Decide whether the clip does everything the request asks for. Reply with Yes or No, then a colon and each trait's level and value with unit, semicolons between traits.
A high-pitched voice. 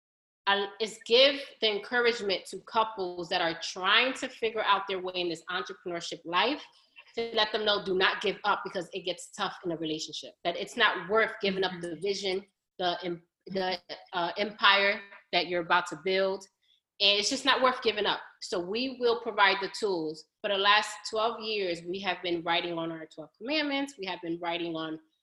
Yes: high, 195 Hz